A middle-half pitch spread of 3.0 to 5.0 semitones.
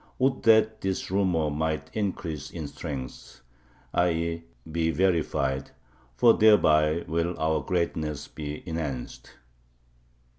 Yes: average, 3.3 semitones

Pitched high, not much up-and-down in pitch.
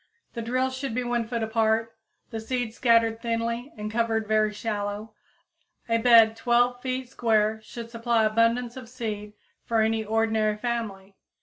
Yes: high, 230 Hz; narrow, 1.5 semitones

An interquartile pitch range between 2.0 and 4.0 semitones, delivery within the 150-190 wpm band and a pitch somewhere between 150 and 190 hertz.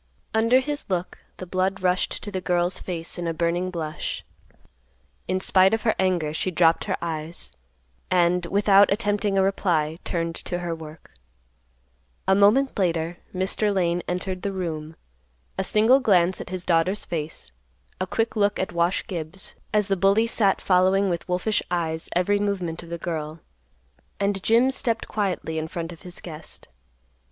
Yes: average, 2.9 semitones; average, 165 wpm; medium, 185 Hz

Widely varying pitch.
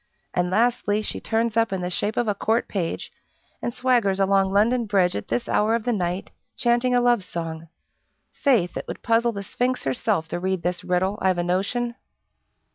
No: average, 4.7 semitones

